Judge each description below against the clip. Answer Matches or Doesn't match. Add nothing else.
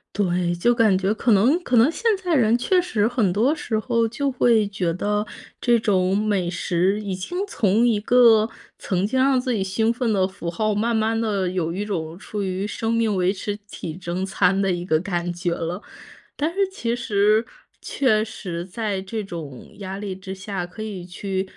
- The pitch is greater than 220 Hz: Doesn't match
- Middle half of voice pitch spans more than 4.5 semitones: Doesn't match